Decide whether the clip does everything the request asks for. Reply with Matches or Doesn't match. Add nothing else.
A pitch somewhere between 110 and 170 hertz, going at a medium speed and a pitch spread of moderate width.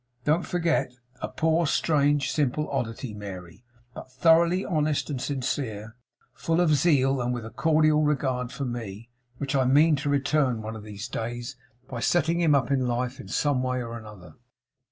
Matches